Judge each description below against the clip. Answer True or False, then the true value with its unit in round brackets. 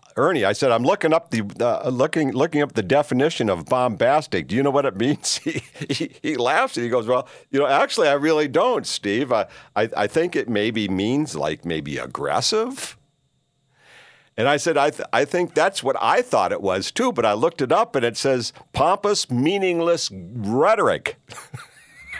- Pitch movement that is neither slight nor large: False (6.2 semitones)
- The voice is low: True (125 Hz)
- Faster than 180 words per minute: True (190 wpm)